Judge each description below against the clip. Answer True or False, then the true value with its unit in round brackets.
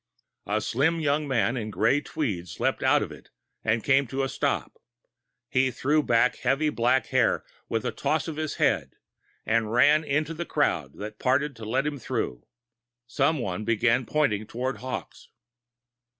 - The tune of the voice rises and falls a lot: False (4.4 semitones)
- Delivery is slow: False (165 wpm)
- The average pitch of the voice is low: True (130 Hz)